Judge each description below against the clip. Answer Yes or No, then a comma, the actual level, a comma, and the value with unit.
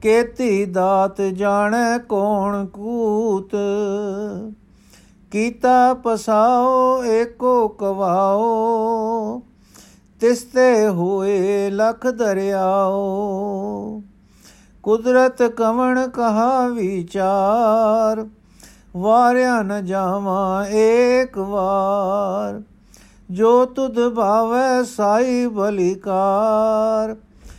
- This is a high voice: Yes, high, 215 Hz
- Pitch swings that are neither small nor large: Yes, average, 3.1 semitones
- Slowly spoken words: Yes, slow, 60 wpm